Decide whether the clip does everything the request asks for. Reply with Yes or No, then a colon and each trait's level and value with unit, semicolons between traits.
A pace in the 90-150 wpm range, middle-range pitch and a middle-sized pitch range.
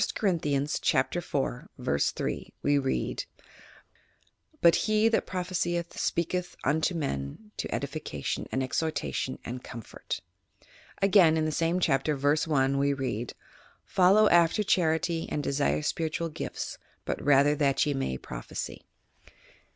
Yes: slow, 135 wpm; medium, 150 Hz; average, 4.1 semitones